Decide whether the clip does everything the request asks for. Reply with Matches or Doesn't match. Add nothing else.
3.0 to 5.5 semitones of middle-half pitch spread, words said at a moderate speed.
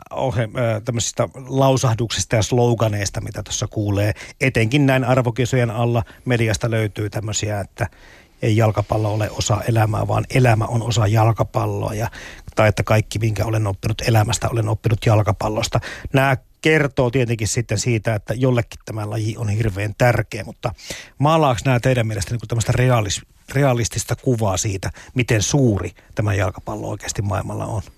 Doesn't match